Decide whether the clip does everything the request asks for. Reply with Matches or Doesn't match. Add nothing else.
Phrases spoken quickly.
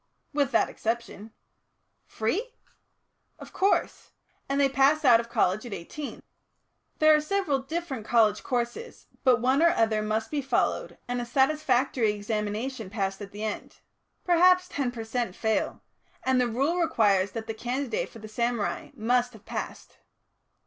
Doesn't match